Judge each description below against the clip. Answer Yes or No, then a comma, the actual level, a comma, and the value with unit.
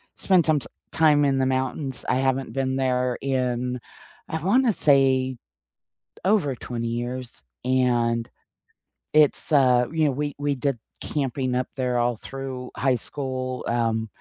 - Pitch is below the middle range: Yes, low, 130 Hz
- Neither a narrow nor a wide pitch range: No, narrow, 2.1 semitones